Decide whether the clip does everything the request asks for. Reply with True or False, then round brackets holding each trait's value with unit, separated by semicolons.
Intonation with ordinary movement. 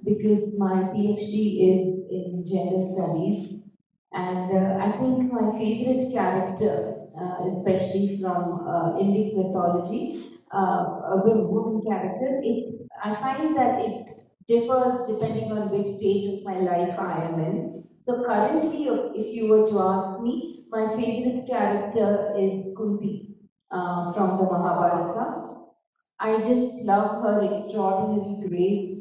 True (3.0 semitones)